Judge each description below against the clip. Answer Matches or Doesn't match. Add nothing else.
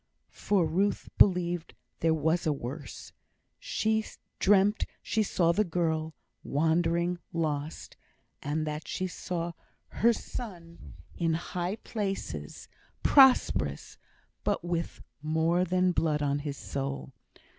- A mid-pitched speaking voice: Matches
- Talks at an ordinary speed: Doesn't match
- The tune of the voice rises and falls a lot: Doesn't match